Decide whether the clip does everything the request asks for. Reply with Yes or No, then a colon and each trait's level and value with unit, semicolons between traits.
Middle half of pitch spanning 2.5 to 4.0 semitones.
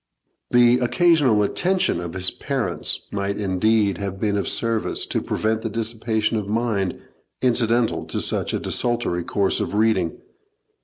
Yes: average, 3.2 semitones